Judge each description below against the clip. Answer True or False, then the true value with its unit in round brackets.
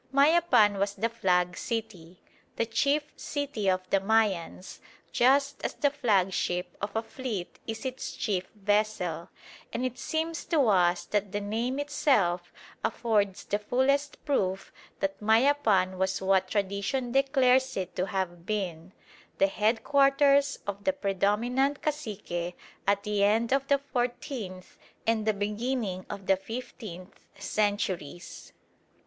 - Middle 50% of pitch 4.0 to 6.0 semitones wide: True (5.3 semitones)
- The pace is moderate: False (130 wpm)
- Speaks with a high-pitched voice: True (210 Hz)